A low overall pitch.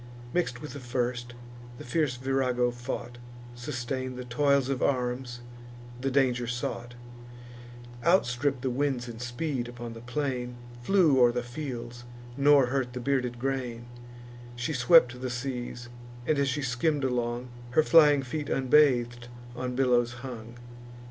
Yes: low, 125 Hz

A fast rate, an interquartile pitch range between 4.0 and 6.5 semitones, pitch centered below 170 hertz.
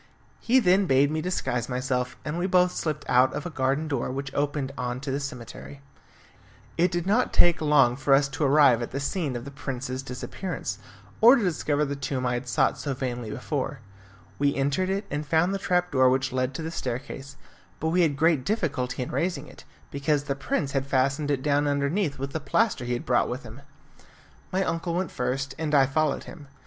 No: fast, 210 wpm; average, 3.5 semitones; medium, 140 Hz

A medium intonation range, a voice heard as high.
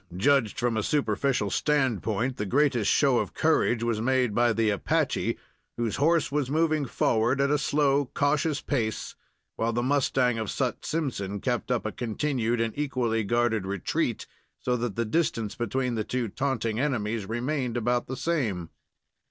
No: average, 3.9 semitones; low, 120 Hz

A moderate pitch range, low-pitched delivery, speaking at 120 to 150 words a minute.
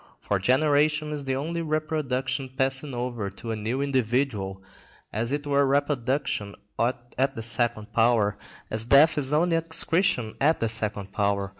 Yes: average, 4.4 semitones; low, 130 Hz; average, 145 wpm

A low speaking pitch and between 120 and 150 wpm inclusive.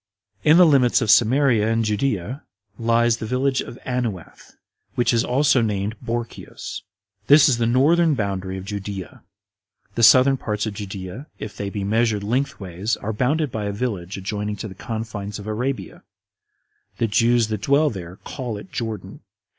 No: low, 115 Hz; average, 160 wpm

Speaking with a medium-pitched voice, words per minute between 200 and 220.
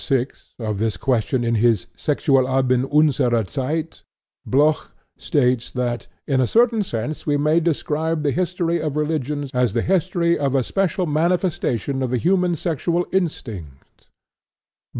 No: medium, 145 Hz; average, 140 wpm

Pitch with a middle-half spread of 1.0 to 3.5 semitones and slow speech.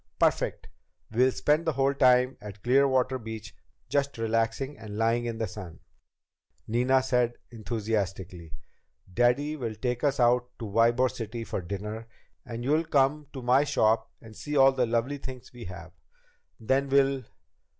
No: average, 3.2 semitones; average, 150 wpm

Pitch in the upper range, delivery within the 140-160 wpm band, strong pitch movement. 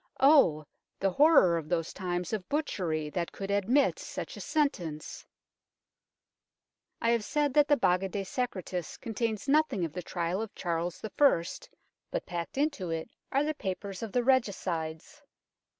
Yes: high, 195 Hz; average, 150 wpm; wide, 7.4 semitones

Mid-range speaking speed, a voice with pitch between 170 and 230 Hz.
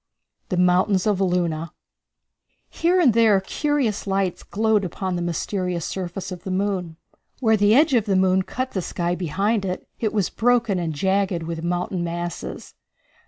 Yes: average, 165 wpm; high, 190 Hz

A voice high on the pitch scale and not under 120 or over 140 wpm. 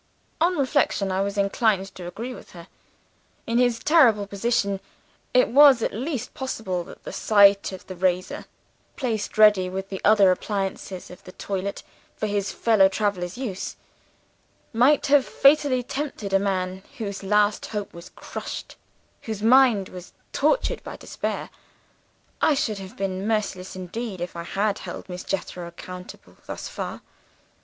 No: high, 200 Hz; average, 150 wpm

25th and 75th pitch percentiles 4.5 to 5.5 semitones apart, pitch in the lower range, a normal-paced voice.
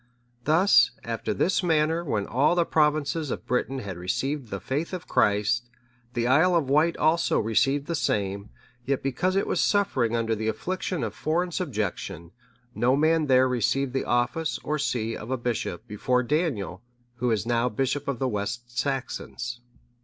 Yes: average, 5.1 semitones; low, 130 Hz; average, 170 wpm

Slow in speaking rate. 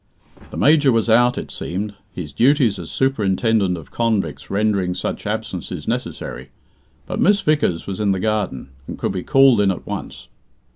No: average, 165 wpm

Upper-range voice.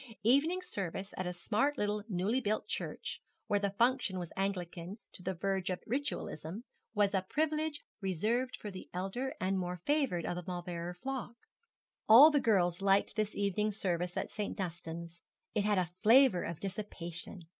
Yes: high, 195 Hz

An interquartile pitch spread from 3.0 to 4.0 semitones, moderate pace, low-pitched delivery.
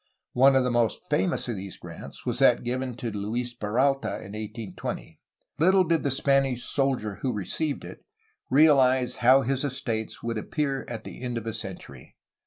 Yes: average, 3.6 semitones; average, 175 wpm; low, 125 Hz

